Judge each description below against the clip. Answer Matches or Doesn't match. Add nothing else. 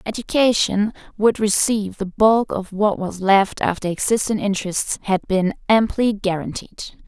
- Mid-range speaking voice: Doesn't match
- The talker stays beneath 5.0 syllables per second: Matches